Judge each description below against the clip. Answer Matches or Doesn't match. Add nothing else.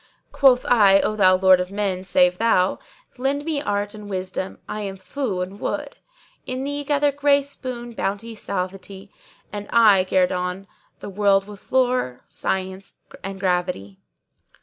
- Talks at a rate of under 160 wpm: Matches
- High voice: Matches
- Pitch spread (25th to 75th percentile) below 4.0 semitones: Doesn't match